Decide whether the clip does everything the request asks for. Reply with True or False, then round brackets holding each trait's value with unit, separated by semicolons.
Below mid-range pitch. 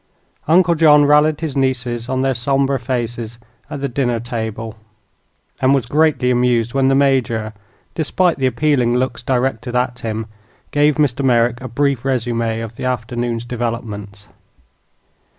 True (125 Hz)